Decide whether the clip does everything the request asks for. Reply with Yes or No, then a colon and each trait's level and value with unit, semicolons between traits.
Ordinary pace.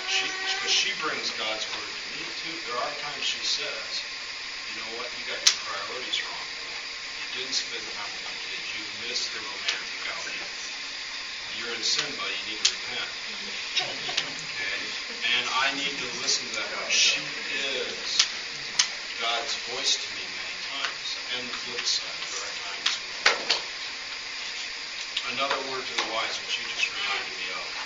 Yes: average, 165 wpm